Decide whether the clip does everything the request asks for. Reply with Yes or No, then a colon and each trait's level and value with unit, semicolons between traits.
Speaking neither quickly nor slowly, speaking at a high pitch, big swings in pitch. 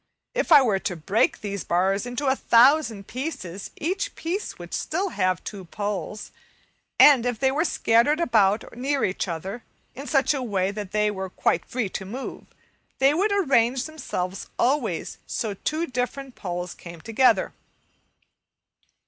Yes: average, 155 wpm; high, 235 Hz; wide, 6.3 semitones